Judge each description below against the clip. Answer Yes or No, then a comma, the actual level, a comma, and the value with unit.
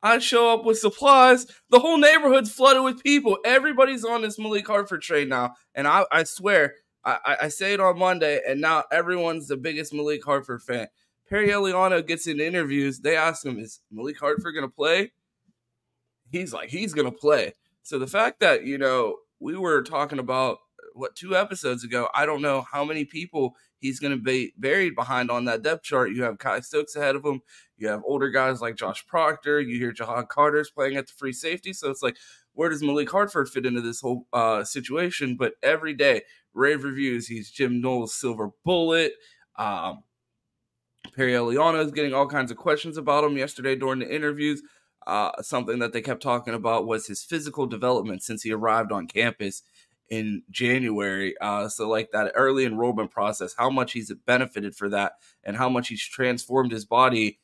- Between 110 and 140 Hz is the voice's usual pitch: Yes, low, 135 Hz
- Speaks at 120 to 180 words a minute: No, average, 195 wpm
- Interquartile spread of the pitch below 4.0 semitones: No, wide, 5.5 semitones